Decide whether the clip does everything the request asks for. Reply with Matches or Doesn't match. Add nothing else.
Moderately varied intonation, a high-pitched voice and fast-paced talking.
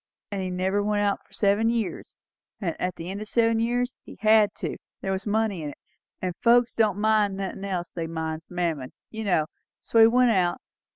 Matches